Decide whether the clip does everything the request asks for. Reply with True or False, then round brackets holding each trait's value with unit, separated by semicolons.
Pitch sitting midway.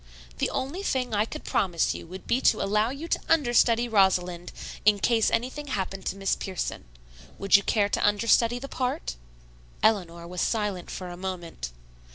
False (205 Hz)